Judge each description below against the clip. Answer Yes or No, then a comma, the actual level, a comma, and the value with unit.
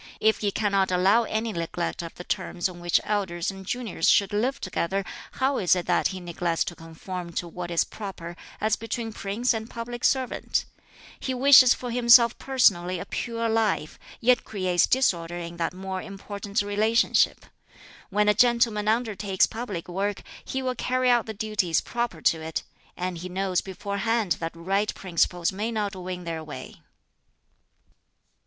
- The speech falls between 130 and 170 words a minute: Yes, average, 165 wpm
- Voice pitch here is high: Yes, high, 200 Hz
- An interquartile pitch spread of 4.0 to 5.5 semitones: Yes, average, 4.3 semitones